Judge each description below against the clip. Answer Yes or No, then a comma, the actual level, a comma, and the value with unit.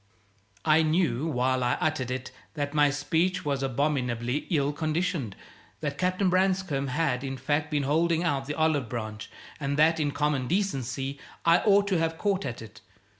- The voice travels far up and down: No, average, 3.6 semitones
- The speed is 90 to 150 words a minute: No, average, 170 wpm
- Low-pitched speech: No, medium, 145 Hz